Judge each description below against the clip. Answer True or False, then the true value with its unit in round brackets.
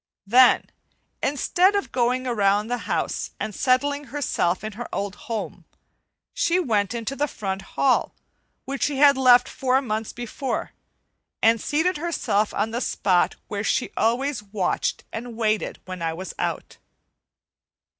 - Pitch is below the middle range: False (240 Hz)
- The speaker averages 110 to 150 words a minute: True (145 wpm)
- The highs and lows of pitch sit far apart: False (4.6 semitones)